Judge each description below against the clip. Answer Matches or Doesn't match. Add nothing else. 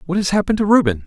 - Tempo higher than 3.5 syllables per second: Matches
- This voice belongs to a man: Matches